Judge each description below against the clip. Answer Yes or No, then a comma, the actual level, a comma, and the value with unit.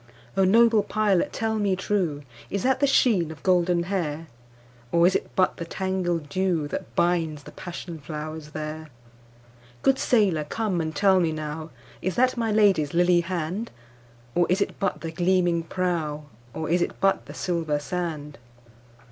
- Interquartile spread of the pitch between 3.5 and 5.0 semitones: Yes, average, 4.1 semitones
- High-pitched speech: No, medium, 170 Hz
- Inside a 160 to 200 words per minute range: No, average, 145 wpm